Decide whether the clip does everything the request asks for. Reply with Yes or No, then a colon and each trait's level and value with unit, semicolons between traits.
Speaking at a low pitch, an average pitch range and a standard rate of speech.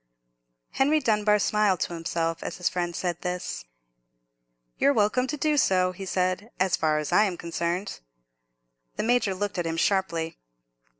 No: medium, 185 Hz; average, 3.6 semitones; average, 160 wpm